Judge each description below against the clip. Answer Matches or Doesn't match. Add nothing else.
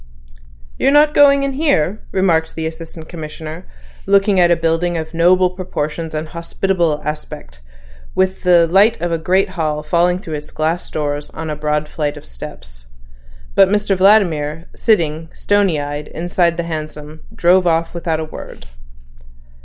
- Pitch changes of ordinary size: Matches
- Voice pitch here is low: Doesn't match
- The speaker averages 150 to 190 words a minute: Matches